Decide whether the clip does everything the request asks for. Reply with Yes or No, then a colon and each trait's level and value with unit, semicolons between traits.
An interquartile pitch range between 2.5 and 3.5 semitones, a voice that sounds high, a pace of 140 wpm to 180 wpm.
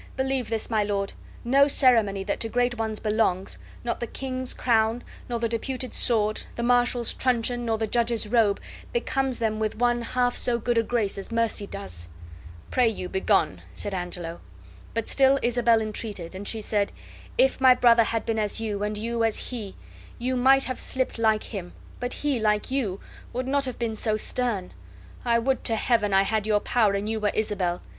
No: average, 2.8 semitones; high, 225 Hz; average, 190 wpm